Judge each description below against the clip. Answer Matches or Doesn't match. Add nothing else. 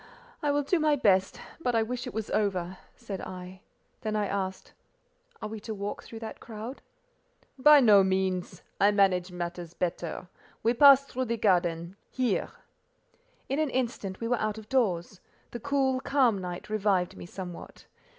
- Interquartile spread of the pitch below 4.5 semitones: Doesn't match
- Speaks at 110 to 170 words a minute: Matches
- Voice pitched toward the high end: Matches